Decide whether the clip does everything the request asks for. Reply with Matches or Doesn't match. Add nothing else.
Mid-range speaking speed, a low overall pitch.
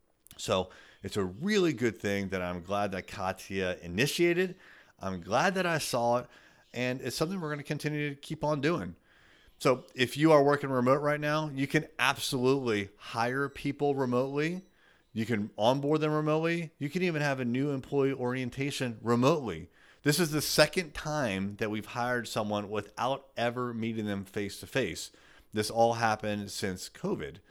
Matches